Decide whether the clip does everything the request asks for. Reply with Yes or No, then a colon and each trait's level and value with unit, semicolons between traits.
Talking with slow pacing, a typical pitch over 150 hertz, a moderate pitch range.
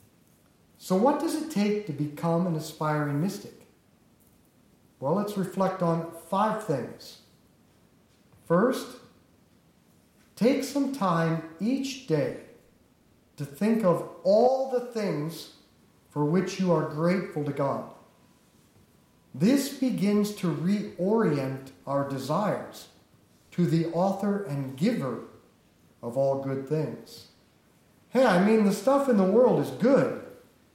No: slow, 115 wpm; medium, 185 Hz; wide, 6.4 semitones